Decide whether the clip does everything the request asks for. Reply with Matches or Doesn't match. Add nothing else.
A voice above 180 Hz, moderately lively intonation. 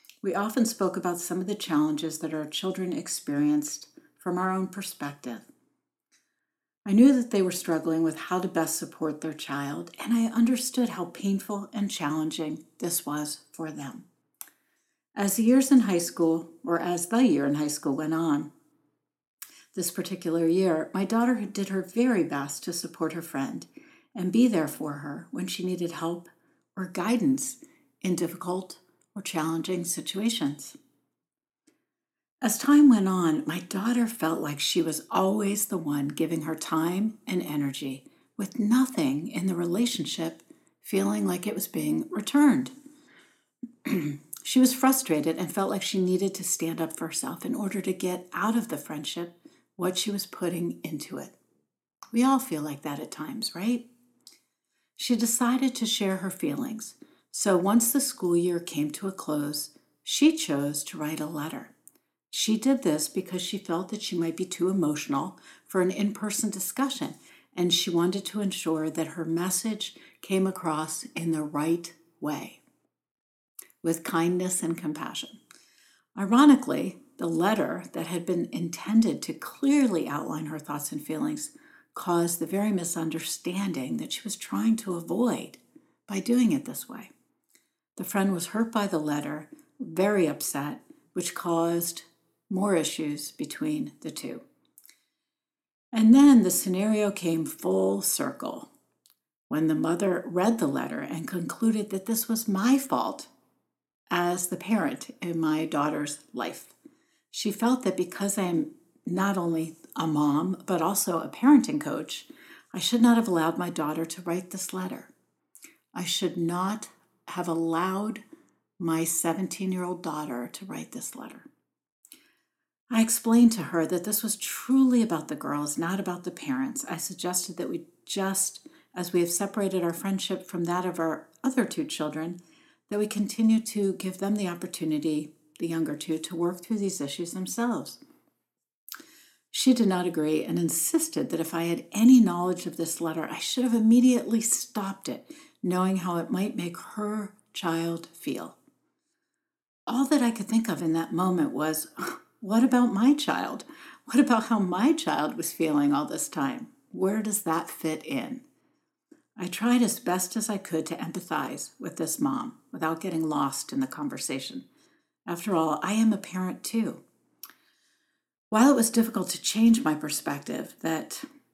Doesn't match